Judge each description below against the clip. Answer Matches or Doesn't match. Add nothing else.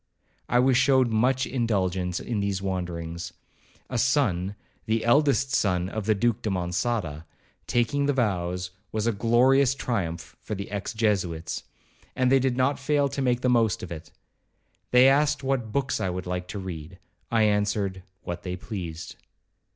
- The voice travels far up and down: Matches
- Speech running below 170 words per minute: Matches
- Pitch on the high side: Doesn't match